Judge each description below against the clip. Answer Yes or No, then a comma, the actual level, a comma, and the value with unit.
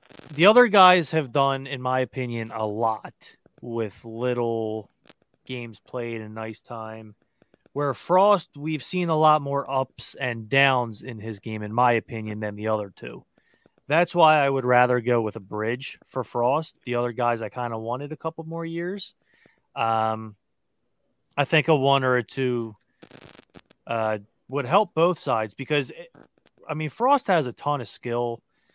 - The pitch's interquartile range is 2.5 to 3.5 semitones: No, average, 5.3 semitones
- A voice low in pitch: Yes, low, 125 Hz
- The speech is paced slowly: No, average, 170 wpm